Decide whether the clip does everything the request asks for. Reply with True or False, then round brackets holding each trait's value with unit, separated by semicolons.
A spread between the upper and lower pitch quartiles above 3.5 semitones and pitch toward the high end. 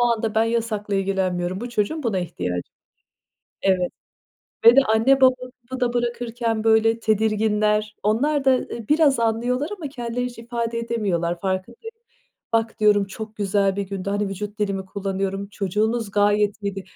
False (3.0 semitones; 215 Hz)